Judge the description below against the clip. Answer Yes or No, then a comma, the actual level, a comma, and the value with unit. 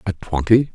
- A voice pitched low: Yes, low, 100 Hz